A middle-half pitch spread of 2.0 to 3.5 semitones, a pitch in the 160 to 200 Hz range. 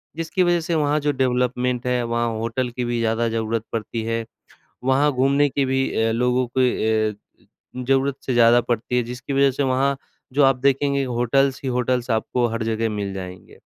No: average, 2.8 semitones; low, 125 Hz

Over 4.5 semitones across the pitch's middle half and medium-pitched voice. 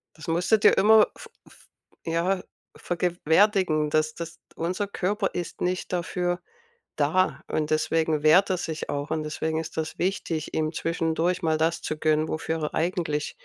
No: average, 2.7 semitones; medium, 165 Hz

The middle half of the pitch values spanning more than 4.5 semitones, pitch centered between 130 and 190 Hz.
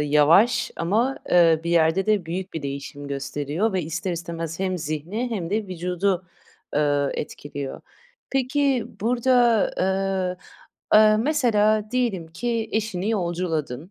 Yes: average, 5.2 semitones; medium, 185 Hz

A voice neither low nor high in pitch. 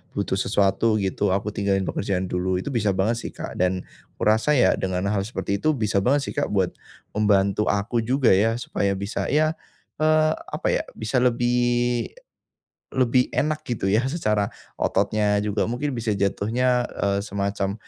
No: low, 105 Hz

